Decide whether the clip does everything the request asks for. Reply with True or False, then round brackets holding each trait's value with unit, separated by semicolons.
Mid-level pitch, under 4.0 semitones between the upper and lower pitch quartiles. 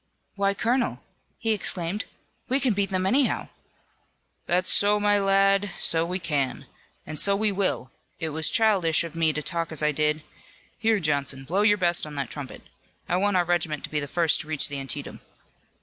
False (175 Hz; 4.8 semitones)